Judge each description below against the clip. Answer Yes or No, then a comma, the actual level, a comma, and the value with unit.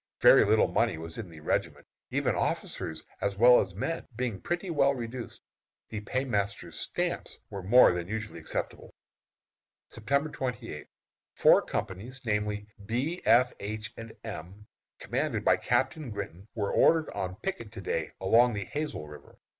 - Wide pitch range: No, average, 4.5 semitones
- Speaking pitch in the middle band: No, low, 110 Hz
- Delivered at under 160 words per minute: Yes, average, 150 wpm